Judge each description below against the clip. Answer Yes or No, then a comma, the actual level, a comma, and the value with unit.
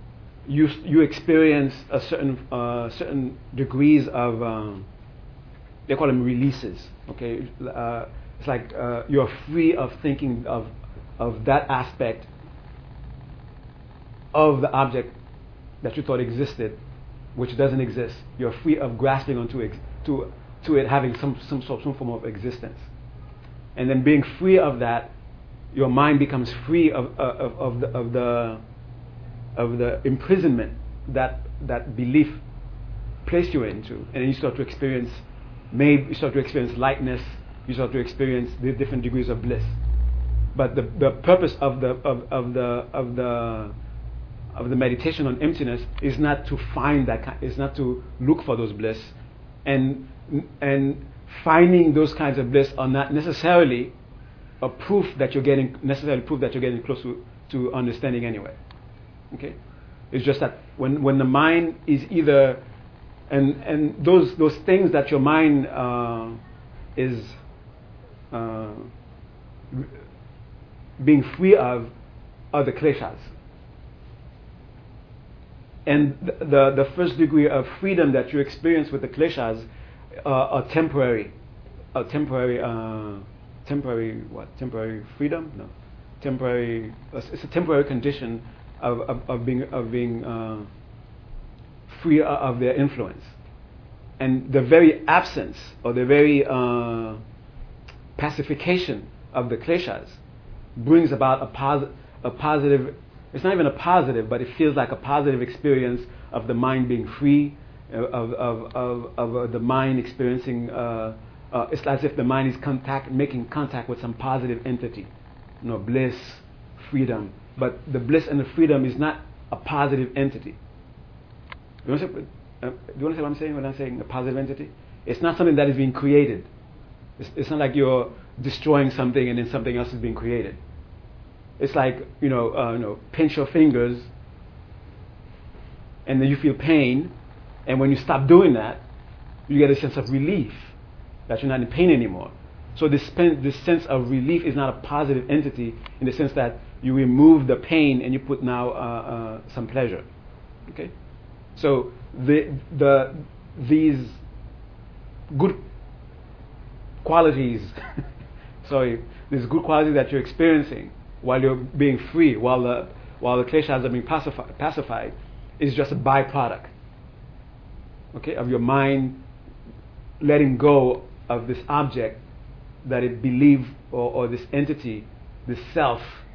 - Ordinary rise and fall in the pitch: Yes, average, 3.0 semitones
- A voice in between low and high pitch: No, low, 130 Hz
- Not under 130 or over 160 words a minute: Yes, average, 150 wpm